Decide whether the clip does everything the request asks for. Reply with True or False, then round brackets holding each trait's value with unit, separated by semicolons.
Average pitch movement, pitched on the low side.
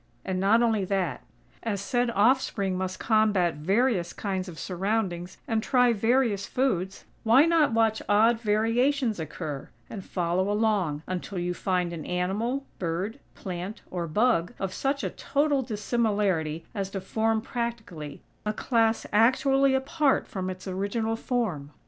False (4.3 semitones; 210 Hz)